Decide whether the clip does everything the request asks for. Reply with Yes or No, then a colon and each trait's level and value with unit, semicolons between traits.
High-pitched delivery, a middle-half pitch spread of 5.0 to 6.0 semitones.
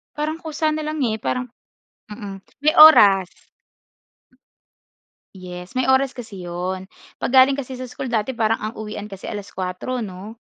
Yes: high, 225 Hz; average, 5.3 semitones